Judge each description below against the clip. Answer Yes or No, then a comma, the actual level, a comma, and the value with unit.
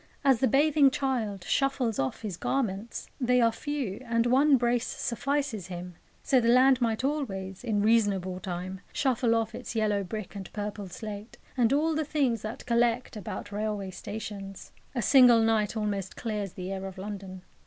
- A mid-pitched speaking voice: No, high, 220 Hz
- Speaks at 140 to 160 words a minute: No, average, 170 wpm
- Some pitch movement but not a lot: Yes, average, 4.2 semitones